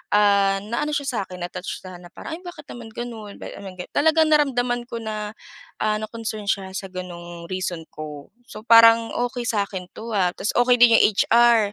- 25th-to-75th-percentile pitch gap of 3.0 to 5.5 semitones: Yes, average, 4.3 semitones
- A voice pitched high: Yes, high, 215 Hz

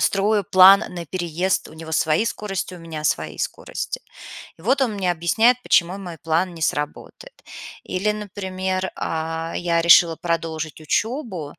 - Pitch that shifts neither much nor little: Yes, average, 3.3 semitones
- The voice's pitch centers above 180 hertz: No, medium, 175 Hz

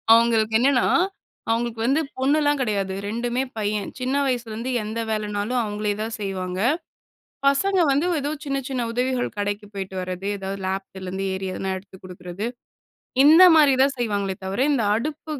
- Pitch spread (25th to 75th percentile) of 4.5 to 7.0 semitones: Yes, average, 4.8 semitones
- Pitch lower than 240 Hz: Yes, high, 220 Hz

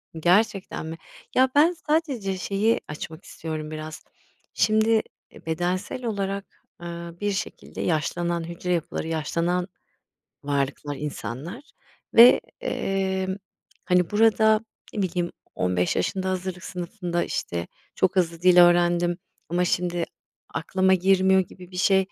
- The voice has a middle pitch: Yes, medium, 180 Hz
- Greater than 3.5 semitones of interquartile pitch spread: No, narrow, 2.6 semitones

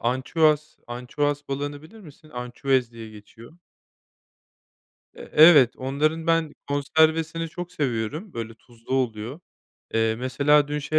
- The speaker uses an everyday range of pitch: Yes, average, 4.2 semitones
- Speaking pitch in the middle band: Yes, medium, 145 Hz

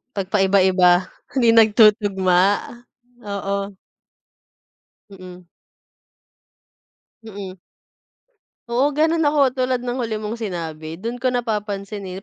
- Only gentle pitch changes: No, average, 4.4 semitones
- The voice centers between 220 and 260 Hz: No, high, 205 Hz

